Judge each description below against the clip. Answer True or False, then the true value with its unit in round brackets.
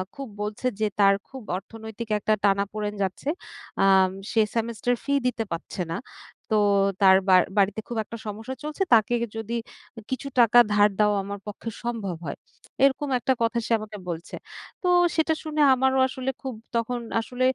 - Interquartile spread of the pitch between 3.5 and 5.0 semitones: True (3.9 semitones)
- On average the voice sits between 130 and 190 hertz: False (225 Hz)